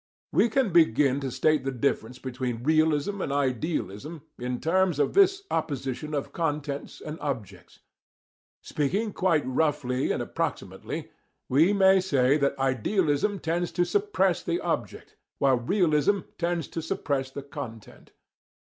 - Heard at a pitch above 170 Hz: No, medium, 150 Hz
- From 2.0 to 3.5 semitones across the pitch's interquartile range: No, average, 4.8 semitones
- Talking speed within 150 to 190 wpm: No, slow, 135 wpm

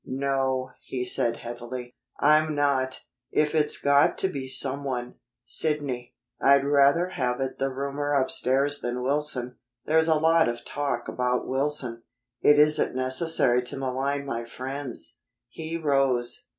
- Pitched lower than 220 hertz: Yes, low, 135 Hz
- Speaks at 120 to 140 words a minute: Yes, slow, 135 wpm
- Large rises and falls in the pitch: No, narrow, 2.5 semitones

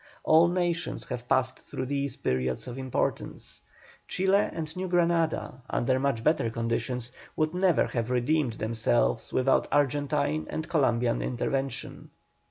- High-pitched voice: No, low, 135 Hz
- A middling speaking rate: No, slow, 130 wpm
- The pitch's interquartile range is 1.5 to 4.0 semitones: No, average, 4.7 semitones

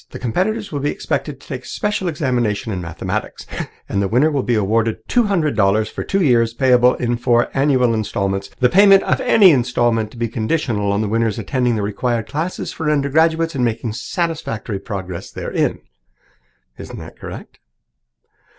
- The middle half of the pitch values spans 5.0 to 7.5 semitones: Yes, wide, 5.6 semitones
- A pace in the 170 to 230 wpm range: Yes, average, 175 wpm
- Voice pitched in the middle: No, low, 120 Hz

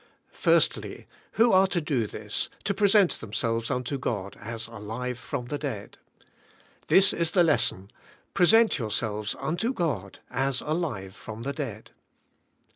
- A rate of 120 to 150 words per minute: Yes, average, 145 wpm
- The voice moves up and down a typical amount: No, wide, 7.8 semitones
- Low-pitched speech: Yes, low, 125 Hz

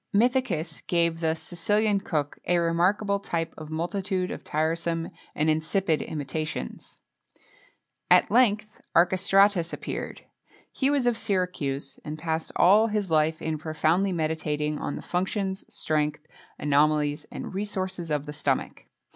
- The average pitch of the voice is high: No, medium, 170 Hz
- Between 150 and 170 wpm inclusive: No, slow, 135 wpm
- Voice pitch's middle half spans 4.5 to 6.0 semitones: No, average, 4.1 semitones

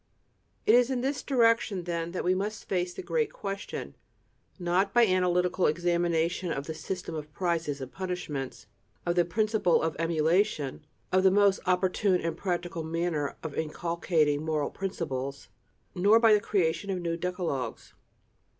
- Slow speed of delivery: No, average, 150 wpm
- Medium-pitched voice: Yes, medium, 175 Hz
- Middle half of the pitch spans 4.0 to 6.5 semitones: No, average, 3.2 semitones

